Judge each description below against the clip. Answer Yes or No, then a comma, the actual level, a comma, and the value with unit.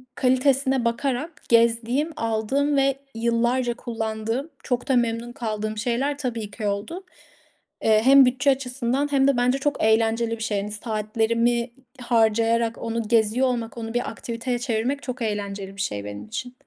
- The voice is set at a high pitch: Yes, high, 235 Hz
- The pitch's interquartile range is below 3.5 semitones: Yes, narrow, 2.6 semitones